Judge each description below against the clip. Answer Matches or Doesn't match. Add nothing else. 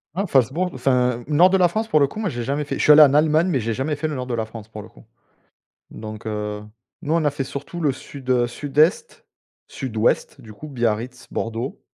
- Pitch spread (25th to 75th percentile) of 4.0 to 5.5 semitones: Matches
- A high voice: Doesn't match